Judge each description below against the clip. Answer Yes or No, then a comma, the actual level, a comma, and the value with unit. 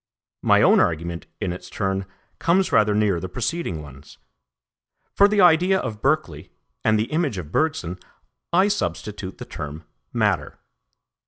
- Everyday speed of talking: Yes, average, 145 wpm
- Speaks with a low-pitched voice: Yes, low, 105 Hz